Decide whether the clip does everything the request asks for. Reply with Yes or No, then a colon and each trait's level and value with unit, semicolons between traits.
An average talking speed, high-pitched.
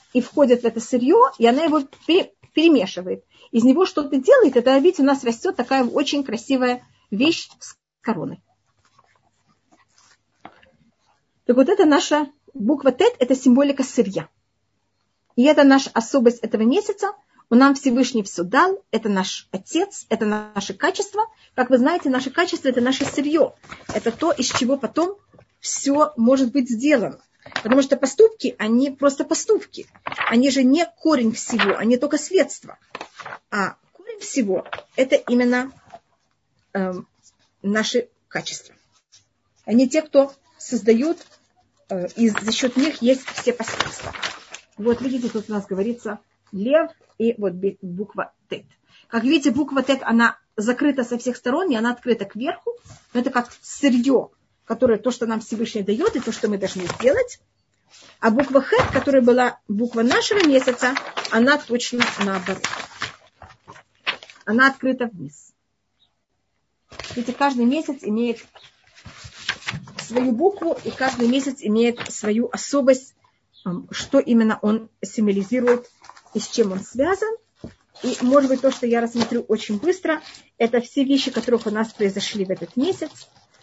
Yes: average, 140 wpm; very high, 250 Hz